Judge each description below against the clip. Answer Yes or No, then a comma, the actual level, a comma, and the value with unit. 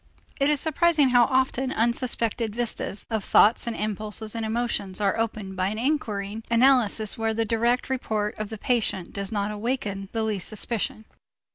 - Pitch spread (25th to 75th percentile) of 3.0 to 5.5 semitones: No, narrow, 2.6 semitones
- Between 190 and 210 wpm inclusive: No, average, 165 wpm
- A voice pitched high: Yes, high, 225 Hz